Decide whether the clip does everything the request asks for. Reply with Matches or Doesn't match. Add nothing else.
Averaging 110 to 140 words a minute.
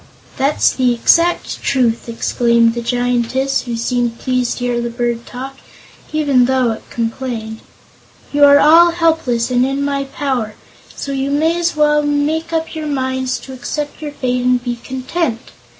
Doesn't match